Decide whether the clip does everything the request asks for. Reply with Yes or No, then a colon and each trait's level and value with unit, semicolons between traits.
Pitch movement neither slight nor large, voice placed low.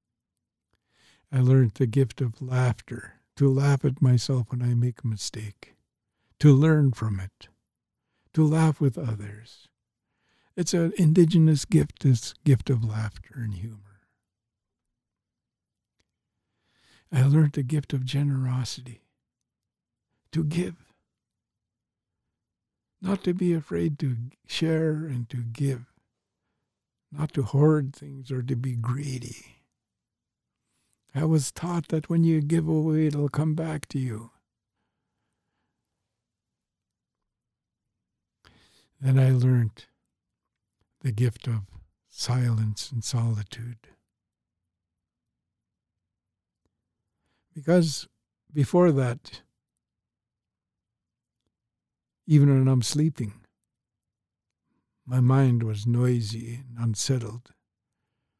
Yes: average, 4.4 semitones; low, 120 Hz